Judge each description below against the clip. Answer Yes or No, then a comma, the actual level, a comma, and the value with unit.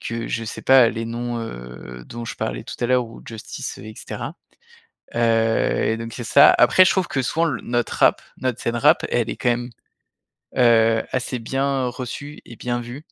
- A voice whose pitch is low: Yes, low, 120 Hz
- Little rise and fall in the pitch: Yes, narrow, 2.0 semitones